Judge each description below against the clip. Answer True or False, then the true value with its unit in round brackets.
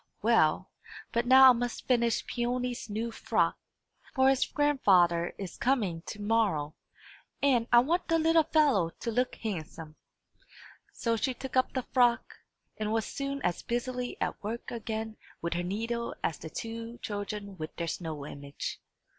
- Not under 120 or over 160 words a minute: True (155 wpm)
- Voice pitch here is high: True (230 Hz)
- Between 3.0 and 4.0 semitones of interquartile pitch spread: False (4.4 semitones)